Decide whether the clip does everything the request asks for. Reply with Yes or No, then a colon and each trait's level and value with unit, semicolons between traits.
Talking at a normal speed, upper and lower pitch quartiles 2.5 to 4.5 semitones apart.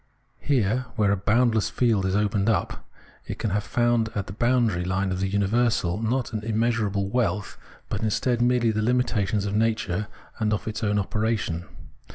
Yes: average, 175 wpm; average, 2.8 semitones